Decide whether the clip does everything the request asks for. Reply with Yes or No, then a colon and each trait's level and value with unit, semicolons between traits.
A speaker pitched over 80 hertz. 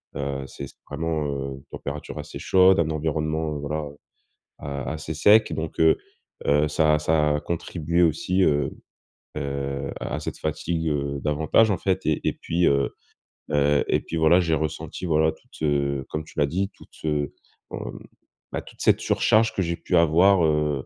No: very low, 75 Hz